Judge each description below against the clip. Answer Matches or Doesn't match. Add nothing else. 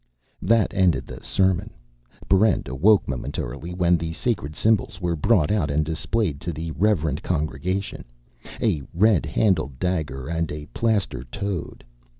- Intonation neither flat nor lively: Matches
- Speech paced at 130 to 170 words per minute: Matches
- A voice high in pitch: Doesn't match